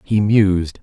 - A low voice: Yes, low, 100 Hz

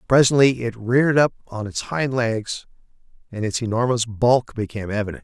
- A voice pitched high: No, low, 120 Hz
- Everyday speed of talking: Yes, average, 160 wpm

